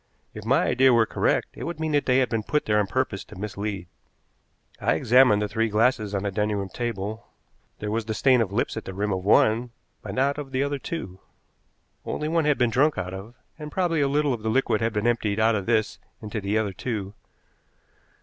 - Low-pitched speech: Yes, low, 110 Hz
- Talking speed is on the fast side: Yes, fast, 225 wpm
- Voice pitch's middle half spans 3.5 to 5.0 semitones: Yes, average, 4.2 semitones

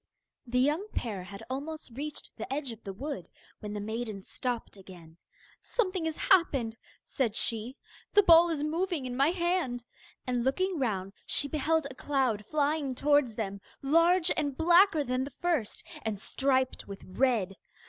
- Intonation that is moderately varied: No, wide, 6.1 semitones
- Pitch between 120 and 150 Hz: No, very high, 265 Hz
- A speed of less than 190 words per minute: Yes, average, 160 wpm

